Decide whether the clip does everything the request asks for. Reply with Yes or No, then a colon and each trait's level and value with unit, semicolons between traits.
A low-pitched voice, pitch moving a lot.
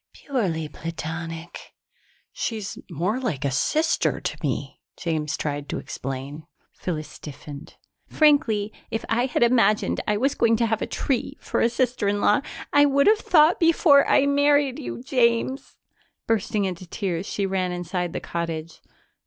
No: high, 210 Hz; wide, 7.8 semitones